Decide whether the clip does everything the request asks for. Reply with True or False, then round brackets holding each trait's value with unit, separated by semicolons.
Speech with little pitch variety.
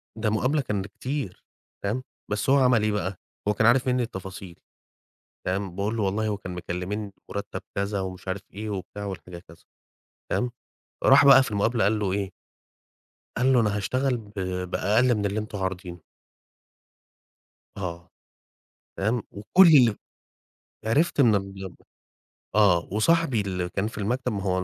False (3.6 semitones)